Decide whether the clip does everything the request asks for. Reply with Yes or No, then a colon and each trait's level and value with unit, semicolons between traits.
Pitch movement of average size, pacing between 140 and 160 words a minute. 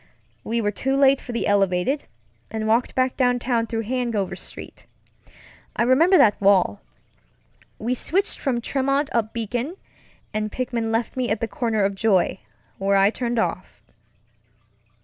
Yes: average, 3.3 semitones; average, 150 wpm